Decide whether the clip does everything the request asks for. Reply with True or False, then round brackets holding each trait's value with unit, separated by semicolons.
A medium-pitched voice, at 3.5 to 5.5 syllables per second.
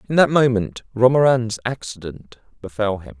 False (115 Hz; 4.9 syllables/s)